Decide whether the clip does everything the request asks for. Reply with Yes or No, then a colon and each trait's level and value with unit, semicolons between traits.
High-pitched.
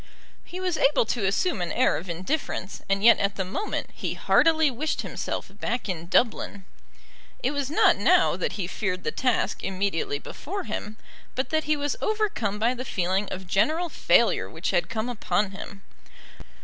Yes: high, 225 Hz